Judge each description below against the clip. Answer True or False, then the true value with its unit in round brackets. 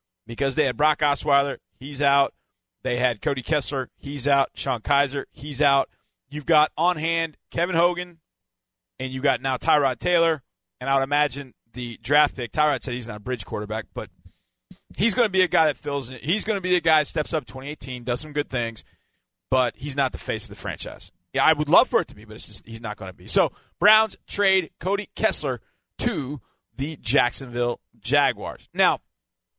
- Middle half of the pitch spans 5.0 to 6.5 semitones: False (4.2 semitones)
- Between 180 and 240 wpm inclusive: True (200 wpm)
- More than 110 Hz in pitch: True (140 Hz)